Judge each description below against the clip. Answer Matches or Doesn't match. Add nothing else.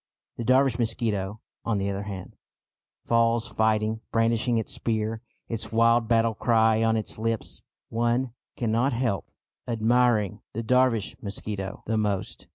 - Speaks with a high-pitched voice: Doesn't match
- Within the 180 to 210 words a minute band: Doesn't match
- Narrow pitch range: Matches